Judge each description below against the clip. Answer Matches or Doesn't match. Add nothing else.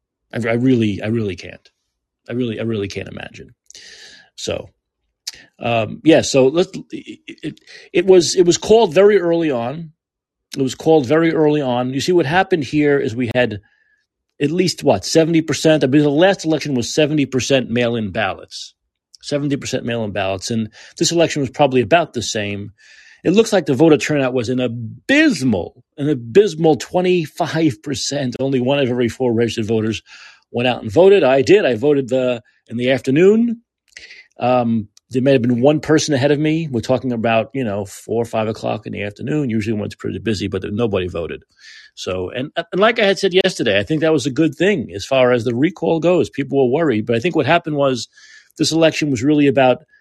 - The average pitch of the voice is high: Doesn't match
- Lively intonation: Matches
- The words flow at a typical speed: Matches